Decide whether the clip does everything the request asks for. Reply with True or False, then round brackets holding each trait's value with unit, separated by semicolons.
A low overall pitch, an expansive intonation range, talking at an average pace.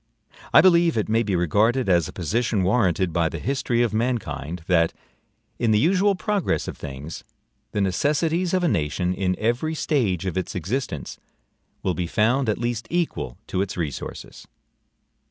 True (110 Hz; 7.1 semitones; 165 wpm)